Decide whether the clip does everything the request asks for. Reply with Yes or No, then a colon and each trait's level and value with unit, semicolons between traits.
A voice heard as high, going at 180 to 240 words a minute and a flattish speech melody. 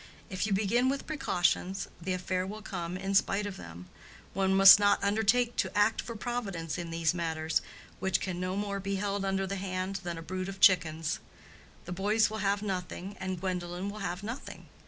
Yes: high, 195 Hz; average, 195 wpm; narrow, 2.2 semitones